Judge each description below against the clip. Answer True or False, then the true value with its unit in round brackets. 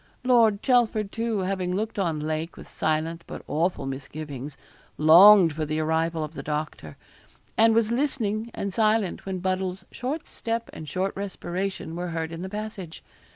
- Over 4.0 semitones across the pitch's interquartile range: True (5.1 semitones)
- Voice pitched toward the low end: False (185 Hz)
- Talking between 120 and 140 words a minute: False (160 wpm)